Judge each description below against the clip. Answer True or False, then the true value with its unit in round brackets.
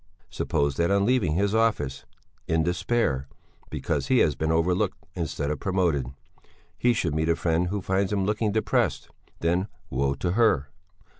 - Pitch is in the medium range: False (90 Hz)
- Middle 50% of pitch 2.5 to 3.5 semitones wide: False (4.7 semitones)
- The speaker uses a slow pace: False (160 wpm)